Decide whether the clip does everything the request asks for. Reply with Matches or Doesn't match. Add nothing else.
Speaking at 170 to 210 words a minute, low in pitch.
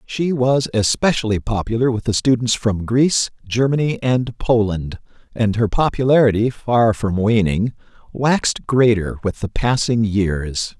Doesn't match